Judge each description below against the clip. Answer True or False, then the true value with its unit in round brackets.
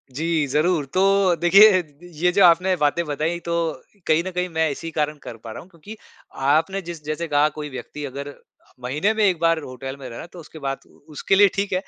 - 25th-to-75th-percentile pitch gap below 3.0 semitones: False (3.7 semitones)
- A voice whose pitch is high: False (165 Hz)